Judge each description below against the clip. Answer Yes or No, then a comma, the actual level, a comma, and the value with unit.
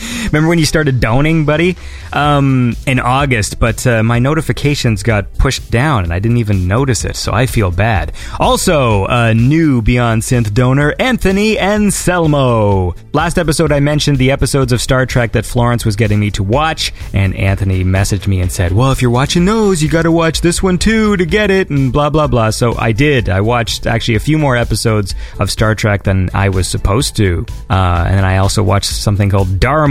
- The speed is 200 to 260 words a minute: Yes, fast, 205 wpm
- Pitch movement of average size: No, wide, 6.4 semitones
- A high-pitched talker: No, low, 120 Hz